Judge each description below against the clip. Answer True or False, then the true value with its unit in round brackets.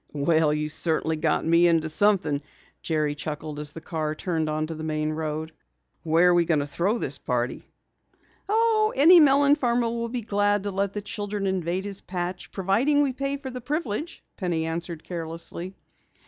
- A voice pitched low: False (175 Hz)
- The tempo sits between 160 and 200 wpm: True (175 wpm)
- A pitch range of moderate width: False (6.4 semitones)